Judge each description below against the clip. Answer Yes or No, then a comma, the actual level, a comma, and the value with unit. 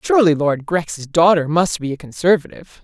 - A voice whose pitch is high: No, medium, 165 Hz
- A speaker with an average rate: Yes, average, 170 wpm